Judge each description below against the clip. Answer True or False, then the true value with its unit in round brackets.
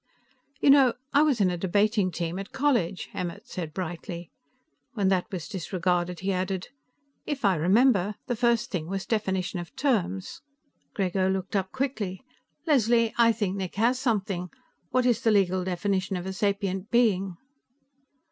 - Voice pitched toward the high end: True (195 Hz)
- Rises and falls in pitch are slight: False (4.0 semitones)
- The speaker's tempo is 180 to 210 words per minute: False (155 wpm)